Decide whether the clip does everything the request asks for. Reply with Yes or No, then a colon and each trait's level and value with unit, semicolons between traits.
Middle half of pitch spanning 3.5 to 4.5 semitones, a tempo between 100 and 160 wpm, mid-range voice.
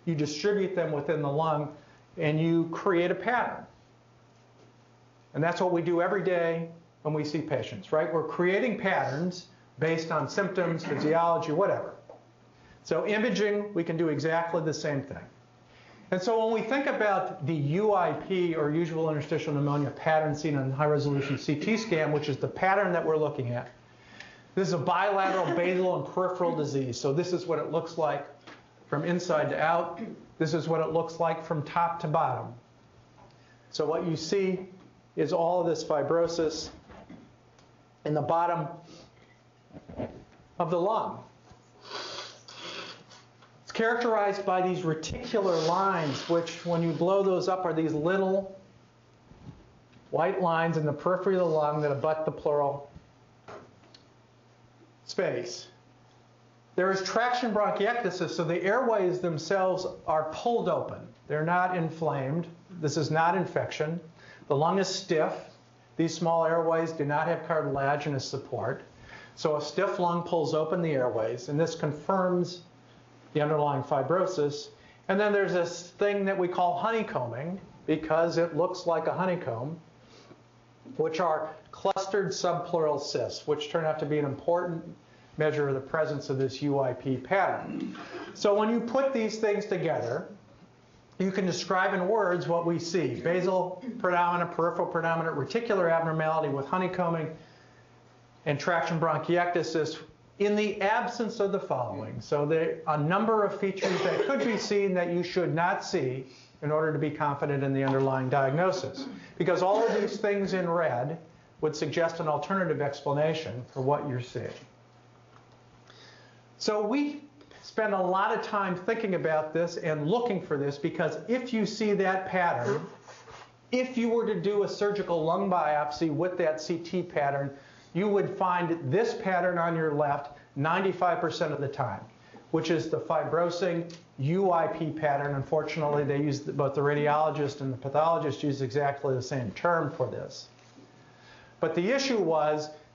Yes: average, 3.9 semitones; average, 155 wpm; medium, 165 Hz